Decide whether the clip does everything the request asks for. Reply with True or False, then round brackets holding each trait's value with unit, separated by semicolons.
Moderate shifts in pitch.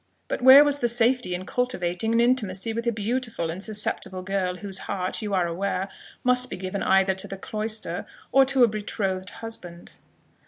True (4.2 semitones)